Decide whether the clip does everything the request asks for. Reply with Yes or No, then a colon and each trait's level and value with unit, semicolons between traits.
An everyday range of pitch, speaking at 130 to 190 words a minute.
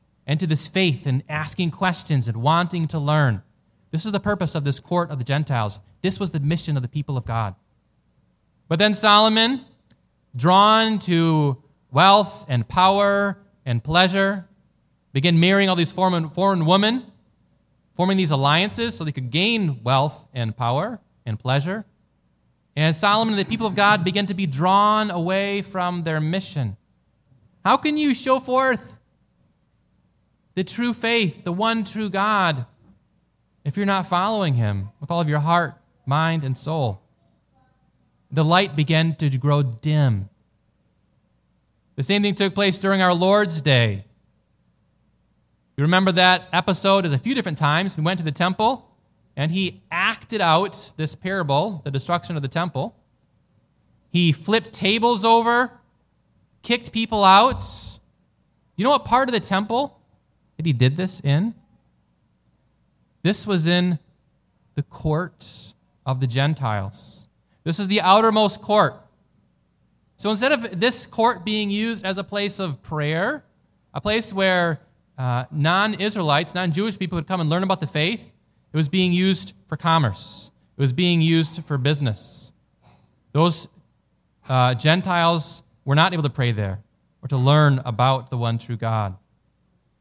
No: wide, 6.1 semitones; average, 150 wpm